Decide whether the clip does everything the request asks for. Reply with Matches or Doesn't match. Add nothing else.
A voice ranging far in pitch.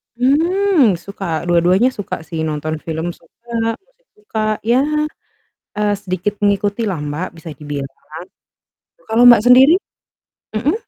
Matches